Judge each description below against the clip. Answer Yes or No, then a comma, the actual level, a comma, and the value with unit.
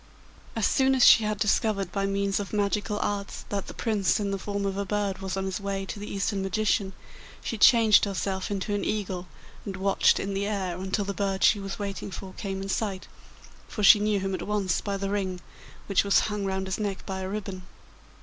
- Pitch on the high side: Yes, high, 200 Hz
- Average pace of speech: No, fast, 220 wpm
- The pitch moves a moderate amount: No, narrow, 1.2 semitones